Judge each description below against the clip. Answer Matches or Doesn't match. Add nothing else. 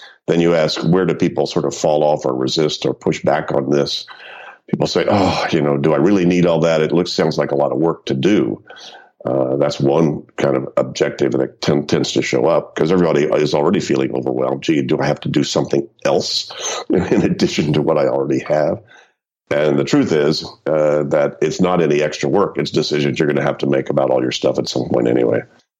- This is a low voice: Matches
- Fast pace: Matches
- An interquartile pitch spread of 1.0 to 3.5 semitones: Matches